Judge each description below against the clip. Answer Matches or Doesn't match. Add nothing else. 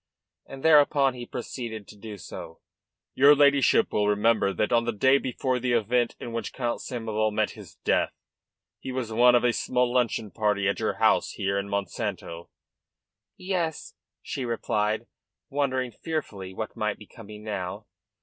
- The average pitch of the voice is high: Doesn't match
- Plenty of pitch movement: Doesn't match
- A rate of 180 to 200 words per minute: Doesn't match